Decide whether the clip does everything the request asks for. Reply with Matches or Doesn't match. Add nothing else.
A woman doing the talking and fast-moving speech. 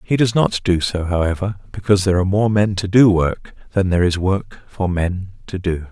Doesn't match